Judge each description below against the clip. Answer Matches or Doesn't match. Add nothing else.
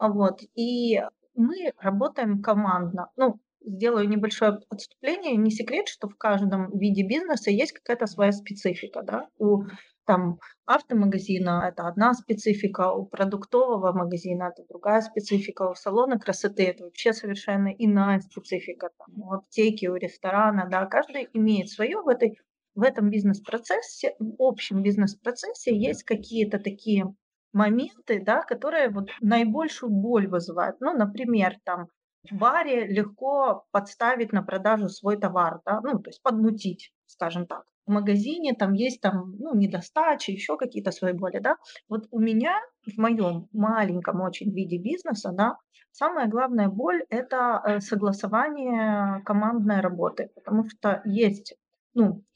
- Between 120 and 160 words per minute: Matches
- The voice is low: Doesn't match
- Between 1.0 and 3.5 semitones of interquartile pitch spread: Matches